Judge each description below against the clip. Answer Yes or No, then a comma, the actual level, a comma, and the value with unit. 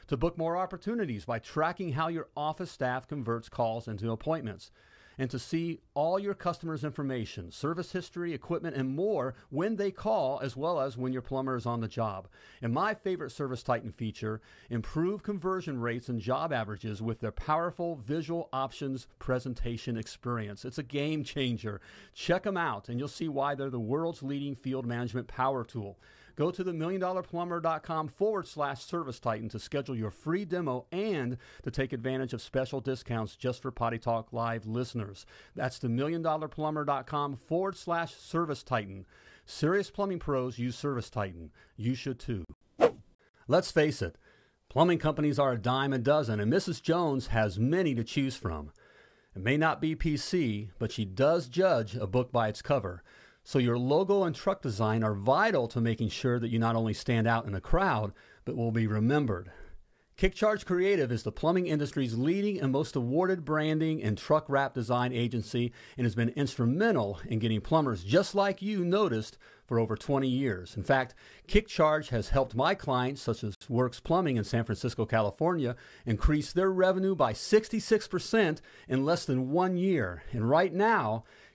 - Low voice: Yes, low, 130 Hz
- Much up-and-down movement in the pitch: Yes, wide, 6.0 semitones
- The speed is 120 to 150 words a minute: No, average, 170 wpm